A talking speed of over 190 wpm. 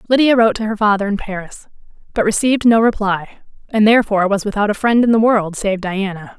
Yes: fast, 205 wpm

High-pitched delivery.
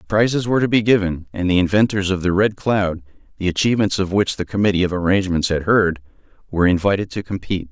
No: very low, 95 Hz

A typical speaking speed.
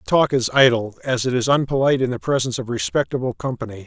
No: fast, 220 wpm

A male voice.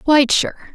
No: female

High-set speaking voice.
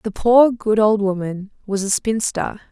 Yes: high, 210 Hz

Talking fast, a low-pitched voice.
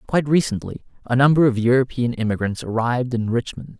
No: average, 160 wpm; low, 125 Hz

